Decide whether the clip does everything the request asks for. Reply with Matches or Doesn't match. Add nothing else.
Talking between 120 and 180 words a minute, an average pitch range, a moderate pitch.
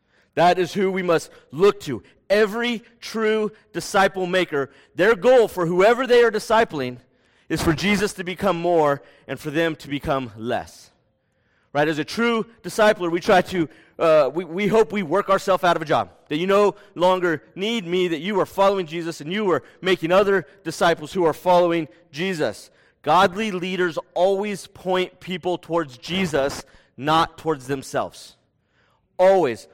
Matches